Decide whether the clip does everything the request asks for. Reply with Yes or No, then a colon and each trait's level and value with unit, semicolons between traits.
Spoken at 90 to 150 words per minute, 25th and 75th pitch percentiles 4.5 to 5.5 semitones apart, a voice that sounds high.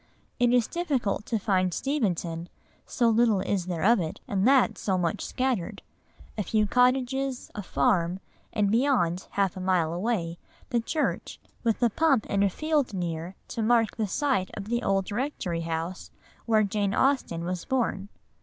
No: average, 165 wpm; average, 5.1 semitones; high, 210 Hz